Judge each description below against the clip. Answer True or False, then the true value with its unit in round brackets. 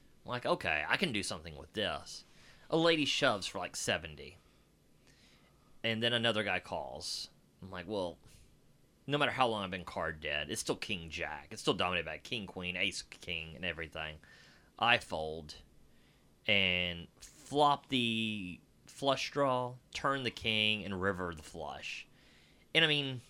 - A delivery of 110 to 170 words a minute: True (155 wpm)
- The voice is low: True (105 Hz)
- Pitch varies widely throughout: True (6.7 semitones)